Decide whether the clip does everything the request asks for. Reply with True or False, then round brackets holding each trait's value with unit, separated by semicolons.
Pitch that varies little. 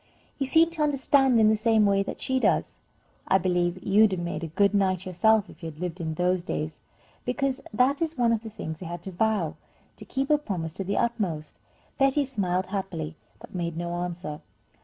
False (5.4 semitones)